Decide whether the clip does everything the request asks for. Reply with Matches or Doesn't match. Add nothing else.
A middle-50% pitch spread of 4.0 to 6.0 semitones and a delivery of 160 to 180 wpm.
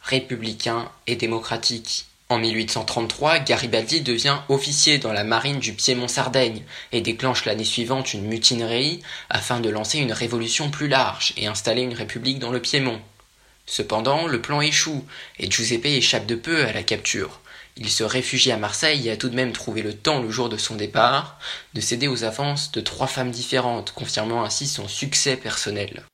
Doesn't match